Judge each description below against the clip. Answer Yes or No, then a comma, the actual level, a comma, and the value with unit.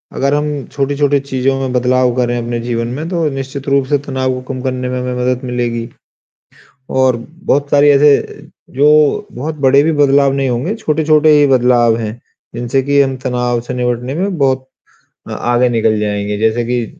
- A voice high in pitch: No, low, 130 Hz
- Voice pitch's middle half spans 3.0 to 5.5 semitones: No, narrow, 2.6 semitones